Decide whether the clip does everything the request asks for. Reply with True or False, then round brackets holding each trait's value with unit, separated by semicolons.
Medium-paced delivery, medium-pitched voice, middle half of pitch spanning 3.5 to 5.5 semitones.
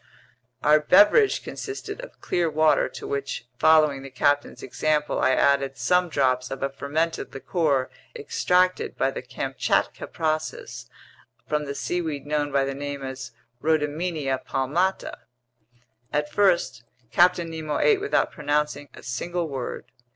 False (130 wpm; 150 Hz; 3.8 semitones)